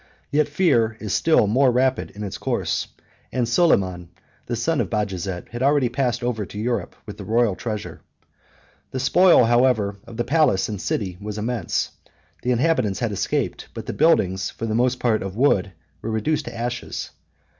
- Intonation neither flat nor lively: Yes, average, 3.9 semitones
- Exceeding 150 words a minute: Yes, average, 175 wpm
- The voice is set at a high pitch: No, low, 120 Hz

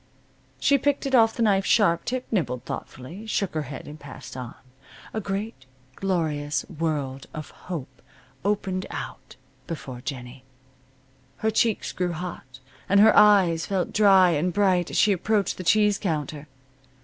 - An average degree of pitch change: No, wide, 5.9 semitones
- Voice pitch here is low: No, medium, 180 Hz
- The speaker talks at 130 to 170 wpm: Yes, average, 150 wpm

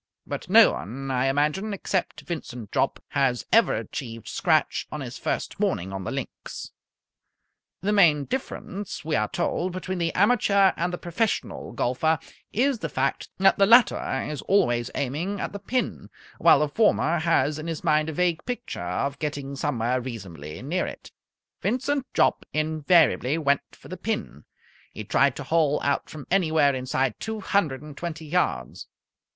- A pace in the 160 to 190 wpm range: Yes, average, 165 wpm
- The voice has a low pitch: No, medium, 155 Hz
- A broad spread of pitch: Yes, wide, 5.8 semitones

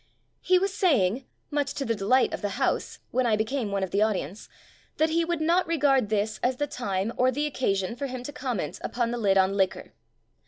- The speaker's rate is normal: No, fast, 225 wpm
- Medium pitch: No, high, 245 Hz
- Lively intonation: Yes, wide, 6.2 semitones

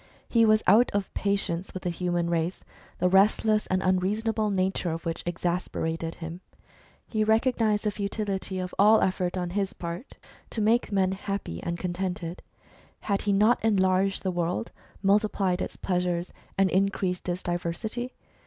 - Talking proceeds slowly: No, average, 155 wpm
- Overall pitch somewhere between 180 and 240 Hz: Yes, high, 190 Hz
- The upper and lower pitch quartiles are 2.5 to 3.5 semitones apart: Yes, average, 2.9 semitones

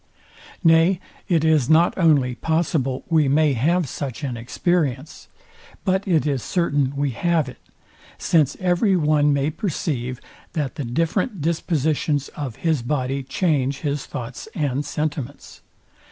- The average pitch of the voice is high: No, medium, 150 Hz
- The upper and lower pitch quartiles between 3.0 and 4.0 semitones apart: Yes, average, 3.6 semitones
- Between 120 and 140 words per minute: Yes, slow, 135 wpm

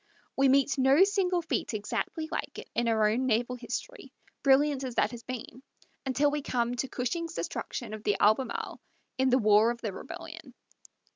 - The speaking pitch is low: No, very high, 255 Hz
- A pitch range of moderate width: Yes, average, 3.9 semitones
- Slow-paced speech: No, average, 180 wpm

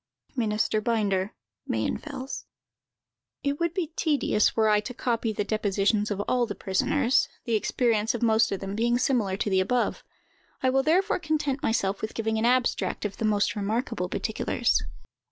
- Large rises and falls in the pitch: No, average, 3.5 semitones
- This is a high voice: Yes, high, 225 Hz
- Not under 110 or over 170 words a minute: Yes, average, 165 wpm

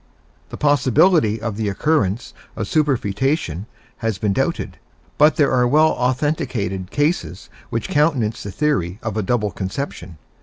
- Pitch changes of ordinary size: No, wide, 6.4 semitones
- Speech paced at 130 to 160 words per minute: Yes, average, 140 wpm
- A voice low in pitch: Yes, low, 120 Hz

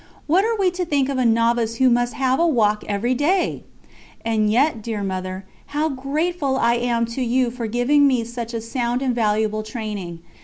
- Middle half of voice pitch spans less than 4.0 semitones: Yes, average, 3.6 semitones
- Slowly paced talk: No, average, 195 wpm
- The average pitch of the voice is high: Yes, high, 240 Hz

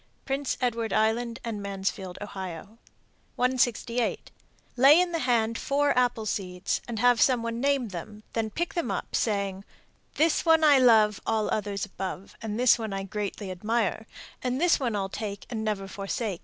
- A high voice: Yes, high, 225 Hz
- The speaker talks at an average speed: Yes, average, 170 wpm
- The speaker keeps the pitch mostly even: No, average, 3.9 semitones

